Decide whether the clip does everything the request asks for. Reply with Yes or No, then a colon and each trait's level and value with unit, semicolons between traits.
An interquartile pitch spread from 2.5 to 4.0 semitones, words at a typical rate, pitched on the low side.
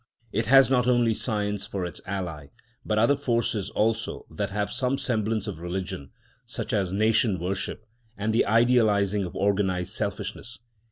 Yes: average, 3.0 semitones; average, 155 wpm; low, 105 Hz